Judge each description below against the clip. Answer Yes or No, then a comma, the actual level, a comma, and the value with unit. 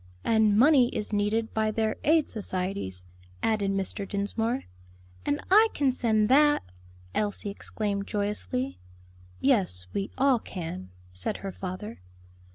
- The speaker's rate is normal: No, slow, 125 wpm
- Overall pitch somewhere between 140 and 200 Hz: No, high, 210 Hz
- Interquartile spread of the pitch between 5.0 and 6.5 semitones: No, average, 2.9 semitones